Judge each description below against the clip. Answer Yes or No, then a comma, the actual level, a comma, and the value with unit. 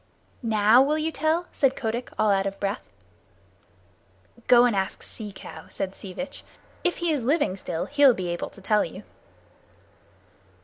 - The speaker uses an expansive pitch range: Yes, wide, 6.4 semitones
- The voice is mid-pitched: No, high, 230 Hz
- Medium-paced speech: Yes, average, 165 wpm